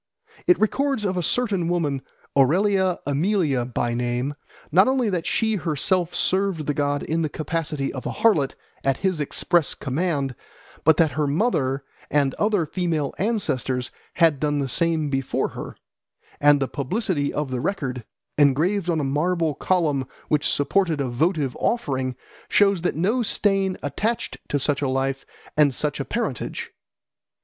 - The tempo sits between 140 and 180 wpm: Yes, average, 155 wpm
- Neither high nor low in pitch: Yes, medium, 155 Hz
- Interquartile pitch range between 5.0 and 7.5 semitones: Yes, average, 5.3 semitones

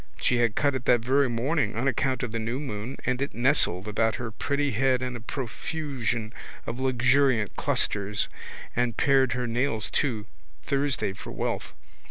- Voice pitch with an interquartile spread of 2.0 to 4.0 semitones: Yes, average, 3.1 semitones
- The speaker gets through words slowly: No, average, 170 wpm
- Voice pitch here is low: Yes, low, 125 Hz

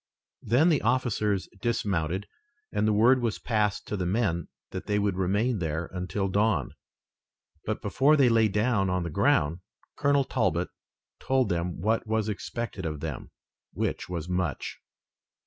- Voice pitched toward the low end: Yes, low, 105 Hz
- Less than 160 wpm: Yes, average, 150 wpm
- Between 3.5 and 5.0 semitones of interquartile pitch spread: Yes, average, 4.4 semitones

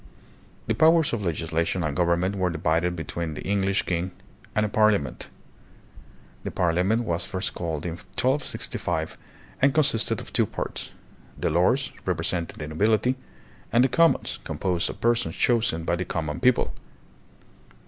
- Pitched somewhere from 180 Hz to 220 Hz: No, very low, 90 Hz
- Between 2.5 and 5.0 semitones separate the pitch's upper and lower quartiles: No, wide, 5.4 semitones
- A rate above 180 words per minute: No, average, 150 wpm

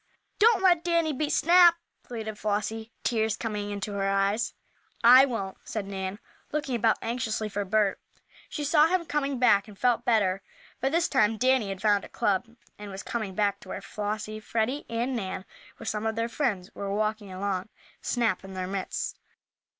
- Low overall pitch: No, high, 220 Hz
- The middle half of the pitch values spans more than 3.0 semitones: Yes, average, 4.0 semitones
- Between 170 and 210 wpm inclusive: Yes, average, 180 wpm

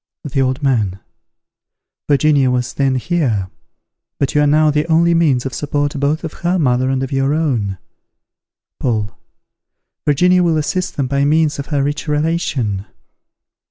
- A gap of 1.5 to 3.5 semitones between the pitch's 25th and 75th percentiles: Yes, average, 3.2 semitones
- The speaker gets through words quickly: No, average, 155 wpm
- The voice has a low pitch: No, medium, 145 Hz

